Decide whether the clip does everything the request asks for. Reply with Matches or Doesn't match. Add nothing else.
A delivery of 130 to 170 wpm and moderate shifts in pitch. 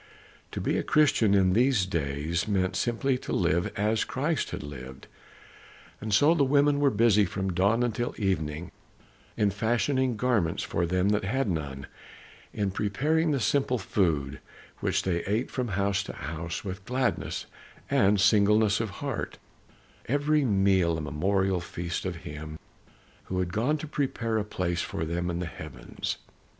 Doesn't match